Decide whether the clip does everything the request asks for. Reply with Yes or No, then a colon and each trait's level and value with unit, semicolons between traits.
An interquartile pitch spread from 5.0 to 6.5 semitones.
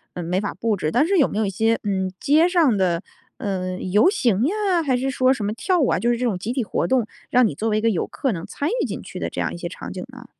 Yes: wide, 5.6 semitones